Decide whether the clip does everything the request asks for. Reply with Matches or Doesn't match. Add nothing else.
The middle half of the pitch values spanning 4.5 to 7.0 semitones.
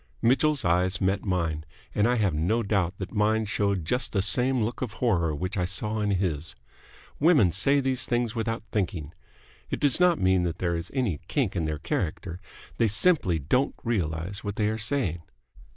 Matches